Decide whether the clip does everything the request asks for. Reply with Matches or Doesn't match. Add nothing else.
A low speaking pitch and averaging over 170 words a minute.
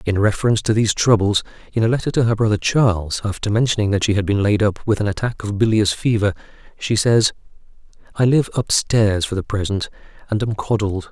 Matches